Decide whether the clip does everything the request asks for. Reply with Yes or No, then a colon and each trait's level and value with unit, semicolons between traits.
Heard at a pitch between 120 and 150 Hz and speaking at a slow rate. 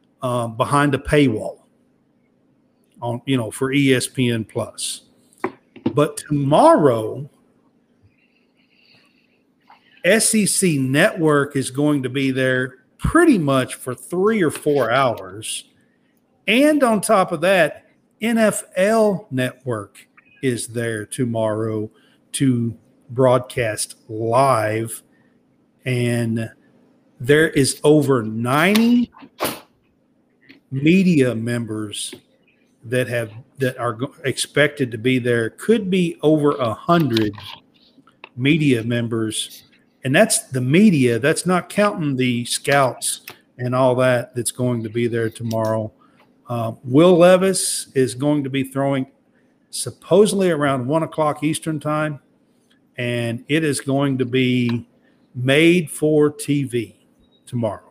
Yes: low, 135 Hz; slow, 105 wpm